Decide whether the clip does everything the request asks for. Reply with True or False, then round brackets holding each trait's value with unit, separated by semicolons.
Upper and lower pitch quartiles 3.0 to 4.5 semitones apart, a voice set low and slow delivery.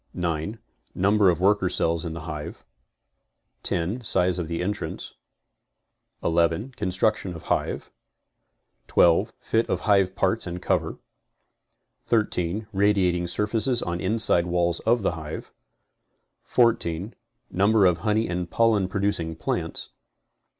True (3.6 semitones; 95 Hz; 115 wpm)